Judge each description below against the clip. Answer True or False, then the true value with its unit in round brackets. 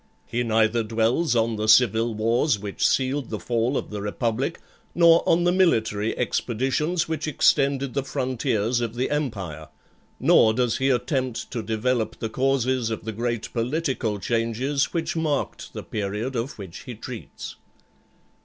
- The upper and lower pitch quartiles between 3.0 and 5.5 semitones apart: True (3.4 semitones)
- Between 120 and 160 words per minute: True (155 wpm)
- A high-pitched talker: False (120 Hz)